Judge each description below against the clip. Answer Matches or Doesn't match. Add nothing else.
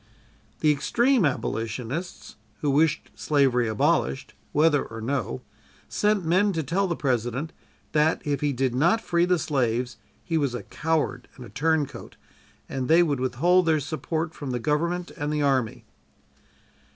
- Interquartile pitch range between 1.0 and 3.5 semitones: Doesn't match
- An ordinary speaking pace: Matches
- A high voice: Doesn't match